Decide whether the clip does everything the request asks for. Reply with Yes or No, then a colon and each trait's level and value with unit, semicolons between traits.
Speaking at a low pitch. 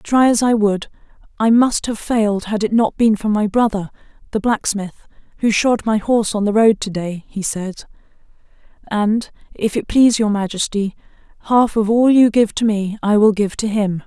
No: high, 215 Hz